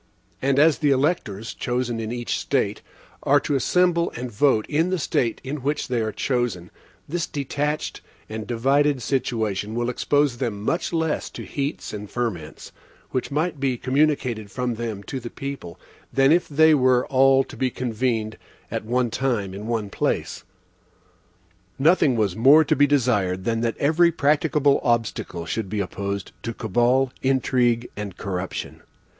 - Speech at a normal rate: Yes, average, 160 wpm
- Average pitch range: Yes, average, 4.4 semitones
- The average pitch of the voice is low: Yes, low, 125 Hz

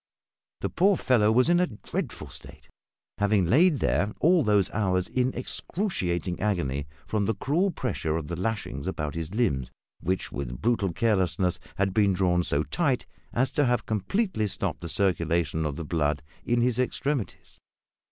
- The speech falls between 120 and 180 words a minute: Yes, average, 160 wpm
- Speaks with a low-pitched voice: Yes, low, 100 Hz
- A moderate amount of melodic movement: No, wide, 6.7 semitones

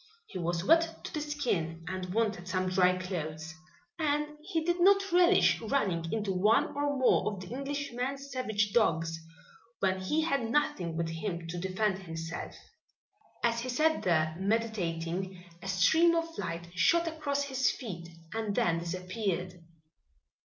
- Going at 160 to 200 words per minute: No, average, 150 wpm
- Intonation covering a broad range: Yes, wide, 8.2 semitones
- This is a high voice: Yes, high, 205 Hz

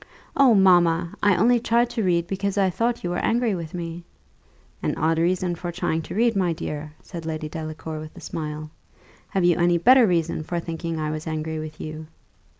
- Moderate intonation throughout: Yes, average, 3.4 semitones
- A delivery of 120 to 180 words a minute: No, average, 200 wpm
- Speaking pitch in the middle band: Yes, medium, 170 Hz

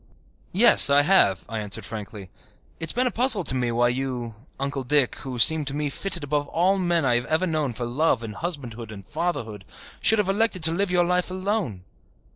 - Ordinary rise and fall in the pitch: No, wide, 7.0 semitones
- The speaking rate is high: Yes, fast, 210 wpm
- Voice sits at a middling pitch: Yes, medium, 145 Hz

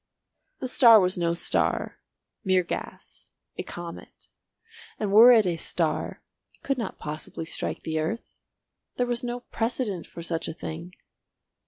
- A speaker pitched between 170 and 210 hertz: Yes, medium, 185 Hz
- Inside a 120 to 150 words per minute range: Yes, average, 140 wpm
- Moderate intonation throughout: No, wide, 5.9 semitones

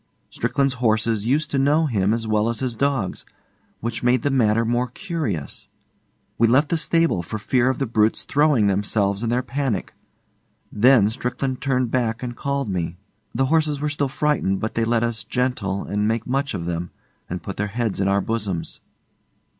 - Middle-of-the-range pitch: No, low, 115 Hz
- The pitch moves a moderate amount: Yes, average, 4.4 semitones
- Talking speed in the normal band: Yes, average, 185 wpm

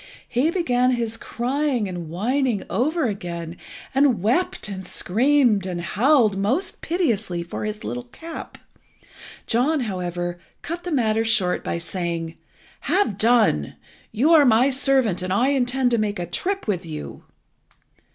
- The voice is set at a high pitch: Yes, high, 225 Hz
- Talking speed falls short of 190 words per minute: Yes, average, 140 wpm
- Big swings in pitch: Yes, wide, 6.5 semitones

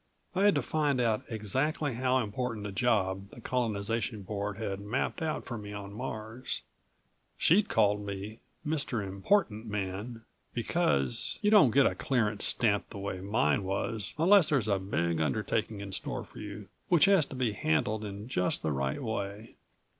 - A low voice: Yes, low, 110 Hz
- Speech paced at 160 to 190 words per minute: Yes, average, 170 wpm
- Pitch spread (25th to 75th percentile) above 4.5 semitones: No, average, 4.2 semitones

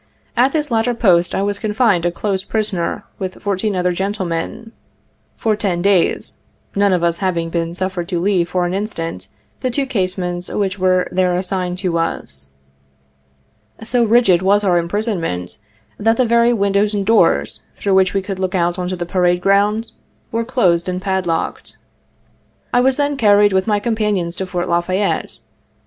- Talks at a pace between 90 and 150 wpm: No, average, 170 wpm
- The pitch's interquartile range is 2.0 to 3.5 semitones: Yes, average, 3.1 semitones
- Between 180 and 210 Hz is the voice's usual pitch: Yes, high, 190 Hz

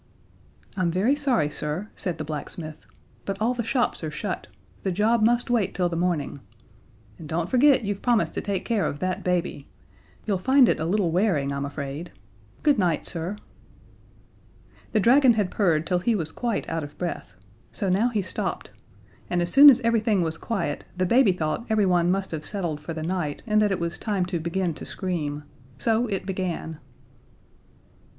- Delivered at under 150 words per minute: No, average, 185 wpm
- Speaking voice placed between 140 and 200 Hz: Yes, medium, 185 Hz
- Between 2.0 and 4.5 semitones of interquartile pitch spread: No, average, 4.9 semitones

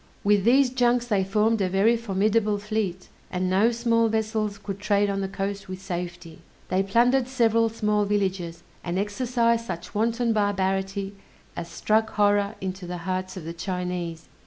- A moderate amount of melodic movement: Yes, average, 3.2 semitones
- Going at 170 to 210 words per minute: No, average, 160 wpm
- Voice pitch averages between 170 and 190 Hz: No, high, 205 Hz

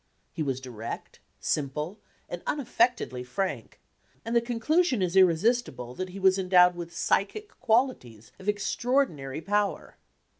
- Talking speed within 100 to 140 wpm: Yes, slow, 135 wpm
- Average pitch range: No, wide, 7.6 semitones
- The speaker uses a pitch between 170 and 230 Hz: Yes, high, 190 Hz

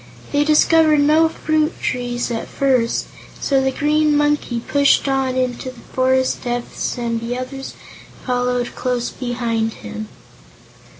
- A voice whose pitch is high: Yes, very high, 255 Hz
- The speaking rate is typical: No, slow, 130 wpm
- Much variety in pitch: No, average, 3.2 semitones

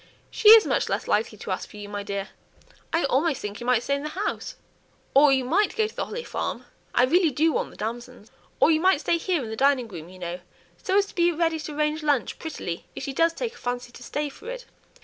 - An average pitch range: No, wide, 6.3 semitones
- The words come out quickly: Yes, fast, 255 wpm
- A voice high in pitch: Yes, very high, 285 Hz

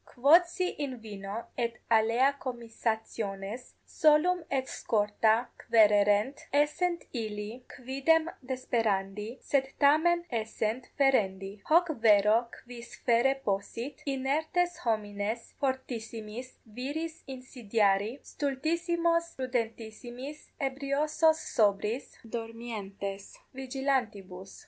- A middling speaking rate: No, slow, 85 wpm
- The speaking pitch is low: No, high, 240 Hz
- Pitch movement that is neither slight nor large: Yes, average, 4.5 semitones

